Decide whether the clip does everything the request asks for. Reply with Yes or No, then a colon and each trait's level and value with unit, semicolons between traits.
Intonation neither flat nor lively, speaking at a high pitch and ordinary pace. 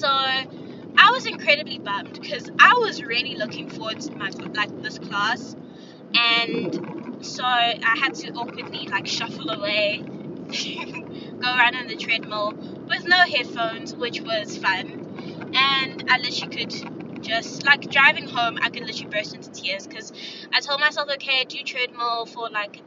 Yes: average, 4.0 semitones; very high, 270 Hz; average, 150 wpm